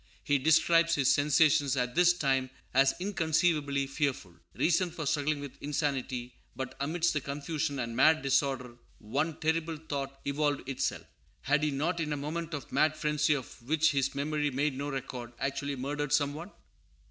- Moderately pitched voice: Yes, medium, 145 Hz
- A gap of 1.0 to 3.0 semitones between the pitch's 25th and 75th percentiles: Yes, narrow, 2.4 semitones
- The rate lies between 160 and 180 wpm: Yes, average, 165 wpm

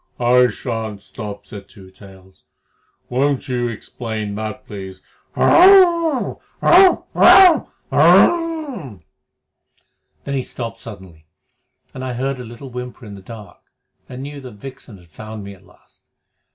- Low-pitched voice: Yes, low, 120 Hz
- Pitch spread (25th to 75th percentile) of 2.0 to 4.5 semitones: No, average, 5.1 semitones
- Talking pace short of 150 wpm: Yes, slow, 135 wpm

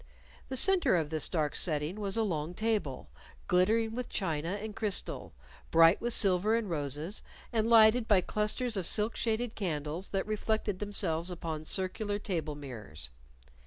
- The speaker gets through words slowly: No, average, 155 wpm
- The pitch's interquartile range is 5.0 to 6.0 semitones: Yes, average, 5.3 semitones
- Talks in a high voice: Yes, high, 195 Hz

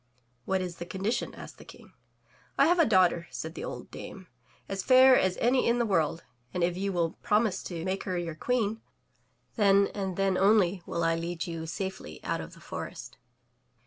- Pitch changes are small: No, average, 3.6 semitones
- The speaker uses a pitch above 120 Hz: Yes, high, 190 Hz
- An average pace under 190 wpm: No, average, 195 wpm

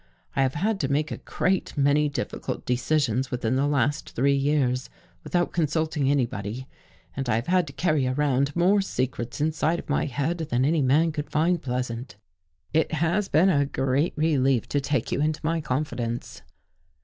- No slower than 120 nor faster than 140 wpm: No, average, 175 wpm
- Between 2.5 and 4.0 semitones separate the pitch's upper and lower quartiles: Yes, average, 3.4 semitones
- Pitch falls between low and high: Yes, medium, 145 Hz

